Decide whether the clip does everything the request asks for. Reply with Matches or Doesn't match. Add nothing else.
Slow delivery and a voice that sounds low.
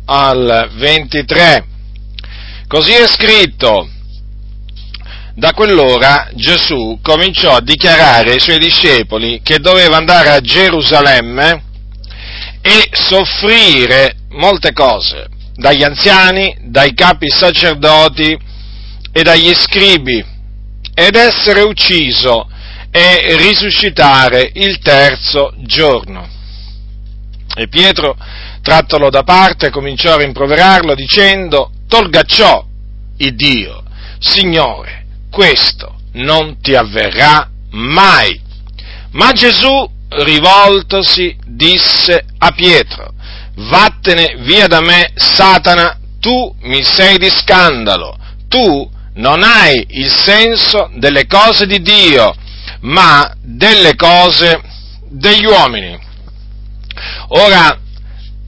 Doesn't match